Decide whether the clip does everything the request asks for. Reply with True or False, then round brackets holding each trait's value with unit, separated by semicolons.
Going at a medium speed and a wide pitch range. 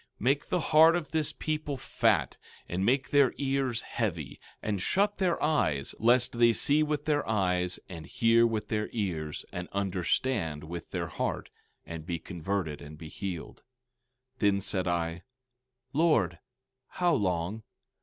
True (150 wpm; 7.9 semitones)